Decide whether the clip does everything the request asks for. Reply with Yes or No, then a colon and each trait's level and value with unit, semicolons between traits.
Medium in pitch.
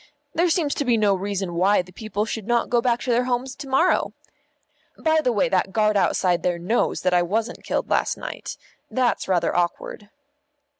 No: high, 215 Hz